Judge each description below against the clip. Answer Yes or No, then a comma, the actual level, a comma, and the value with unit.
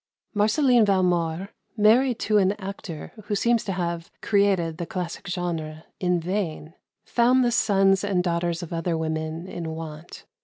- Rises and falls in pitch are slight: No, average, 3.7 semitones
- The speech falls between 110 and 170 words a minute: Yes, average, 150 wpm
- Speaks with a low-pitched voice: No, medium, 180 Hz